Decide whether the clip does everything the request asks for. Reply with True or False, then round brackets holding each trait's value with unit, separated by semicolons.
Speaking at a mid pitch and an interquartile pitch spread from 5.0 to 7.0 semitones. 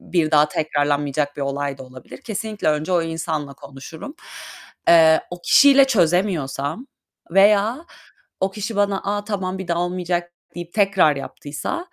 True (175 Hz; 5.3 semitones)